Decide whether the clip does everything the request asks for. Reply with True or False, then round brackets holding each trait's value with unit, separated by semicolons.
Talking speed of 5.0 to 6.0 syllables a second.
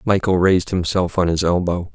True (5.5 syllables/s)